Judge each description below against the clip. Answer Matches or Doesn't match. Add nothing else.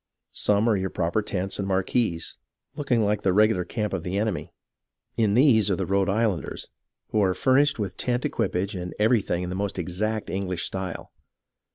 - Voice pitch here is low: Matches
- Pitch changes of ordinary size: Matches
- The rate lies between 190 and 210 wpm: Doesn't match